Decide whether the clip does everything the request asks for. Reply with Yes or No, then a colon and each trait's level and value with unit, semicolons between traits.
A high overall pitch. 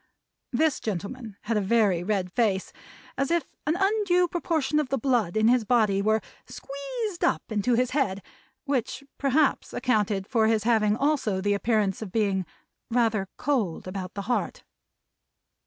Yes: high, 225 Hz